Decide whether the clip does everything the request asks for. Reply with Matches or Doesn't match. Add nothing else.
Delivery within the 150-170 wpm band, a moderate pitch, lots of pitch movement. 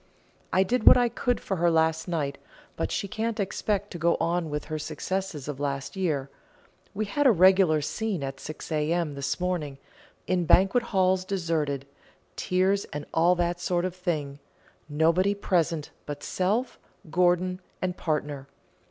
Doesn't match